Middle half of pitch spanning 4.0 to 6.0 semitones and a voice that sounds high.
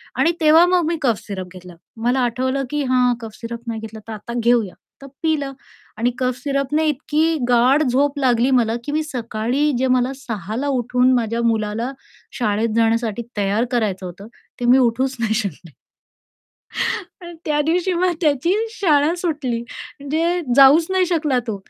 Yes: average, 4.5 semitones; very high, 255 Hz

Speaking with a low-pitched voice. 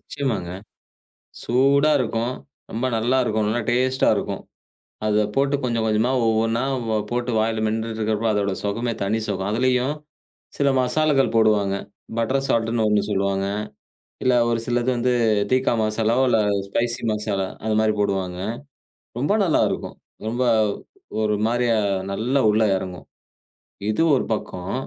Yes: low, 115 Hz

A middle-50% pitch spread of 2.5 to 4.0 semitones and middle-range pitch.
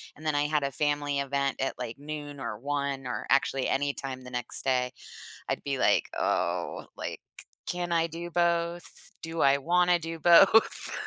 Yes: average, 3.5 semitones; medium, 145 Hz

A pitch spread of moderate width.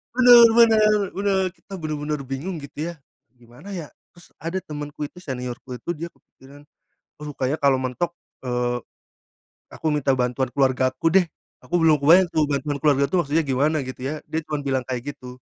Yes: average, 4.3 semitones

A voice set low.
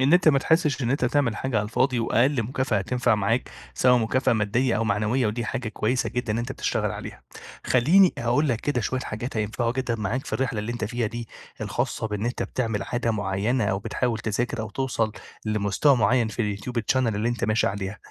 Yes: low, 120 Hz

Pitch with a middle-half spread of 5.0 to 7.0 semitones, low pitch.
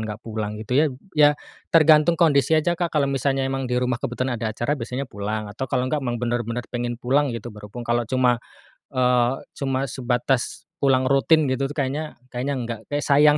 No: average, 2.9 semitones; low, 130 Hz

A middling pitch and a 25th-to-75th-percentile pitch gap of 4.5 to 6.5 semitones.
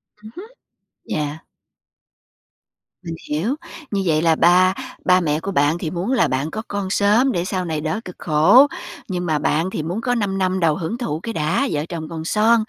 Yes: medium, 180 Hz; average, 4.8 semitones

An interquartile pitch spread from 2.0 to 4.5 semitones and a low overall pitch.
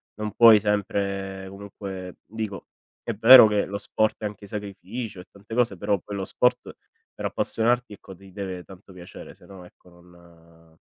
Yes: narrow, 2.5 semitones; low, 100 Hz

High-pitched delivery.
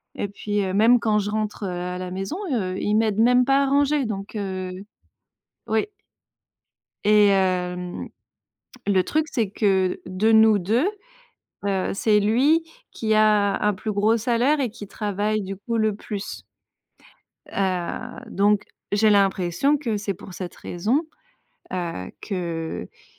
Yes: high, 205 Hz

